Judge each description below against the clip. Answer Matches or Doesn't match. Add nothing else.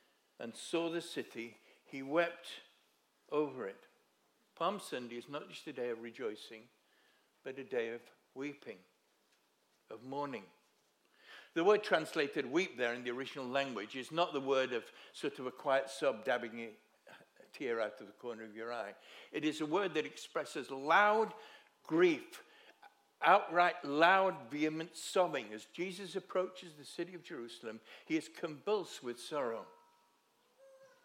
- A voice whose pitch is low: Doesn't match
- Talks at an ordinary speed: Matches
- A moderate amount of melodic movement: Doesn't match